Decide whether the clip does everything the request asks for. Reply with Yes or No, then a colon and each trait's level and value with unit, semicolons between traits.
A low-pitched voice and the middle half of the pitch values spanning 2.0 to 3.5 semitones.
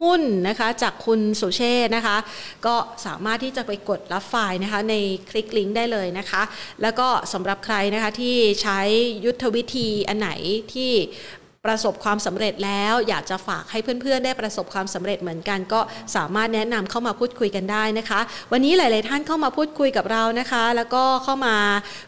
No: high, 220 Hz; average, 3.0 semitones